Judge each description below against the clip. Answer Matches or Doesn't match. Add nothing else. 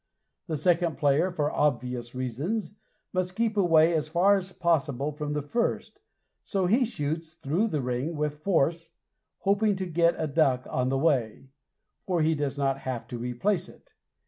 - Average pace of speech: Matches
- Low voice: Doesn't match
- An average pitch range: Matches